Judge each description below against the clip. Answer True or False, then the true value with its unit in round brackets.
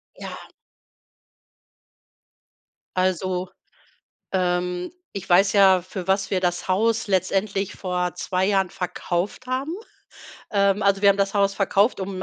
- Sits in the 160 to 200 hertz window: True (190 Hz)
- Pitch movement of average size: False (1.5 semitones)